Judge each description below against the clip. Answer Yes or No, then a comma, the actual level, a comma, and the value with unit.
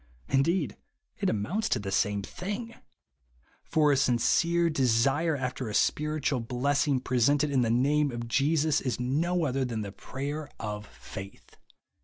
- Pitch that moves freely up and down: No, average, 4.4 semitones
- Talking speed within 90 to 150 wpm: Yes, average, 145 wpm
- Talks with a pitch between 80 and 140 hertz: Yes, low, 135 Hz